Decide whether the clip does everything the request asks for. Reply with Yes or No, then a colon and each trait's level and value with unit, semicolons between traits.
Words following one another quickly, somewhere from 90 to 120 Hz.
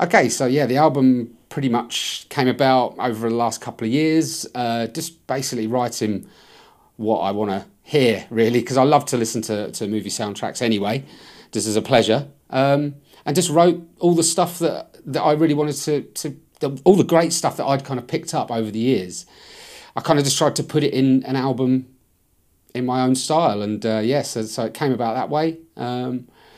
No: fast, 210 wpm; low, 130 Hz